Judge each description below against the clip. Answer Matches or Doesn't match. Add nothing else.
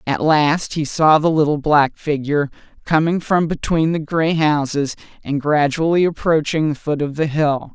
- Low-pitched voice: Doesn't match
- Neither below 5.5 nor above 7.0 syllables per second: Doesn't match